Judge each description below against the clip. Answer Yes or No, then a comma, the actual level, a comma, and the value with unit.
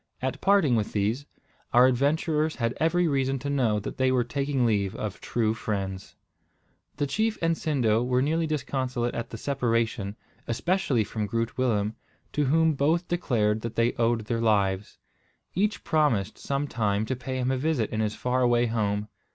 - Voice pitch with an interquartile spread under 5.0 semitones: Yes, average, 4.6 semitones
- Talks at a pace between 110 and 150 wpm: No, average, 170 wpm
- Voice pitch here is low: Yes, low, 125 Hz